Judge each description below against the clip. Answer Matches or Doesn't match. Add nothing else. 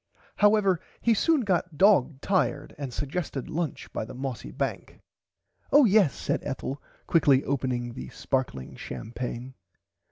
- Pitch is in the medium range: Matches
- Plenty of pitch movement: Matches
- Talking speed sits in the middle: Doesn't match